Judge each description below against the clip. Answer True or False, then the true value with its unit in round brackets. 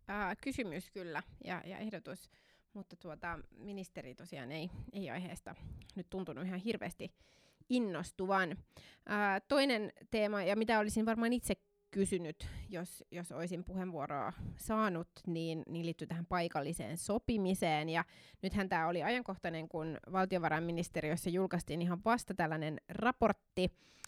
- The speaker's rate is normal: True (125 wpm)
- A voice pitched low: False (185 Hz)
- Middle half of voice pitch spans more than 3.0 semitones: True (3.4 semitones)